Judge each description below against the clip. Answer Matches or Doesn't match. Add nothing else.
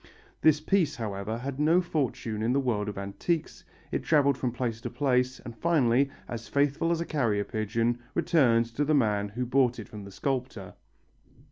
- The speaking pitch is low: Matches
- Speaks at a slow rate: Doesn't match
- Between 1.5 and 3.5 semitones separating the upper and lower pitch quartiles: Doesn't match